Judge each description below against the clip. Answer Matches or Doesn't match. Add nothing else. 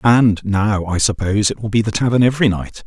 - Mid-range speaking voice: Doesn't match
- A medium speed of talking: Doesn't match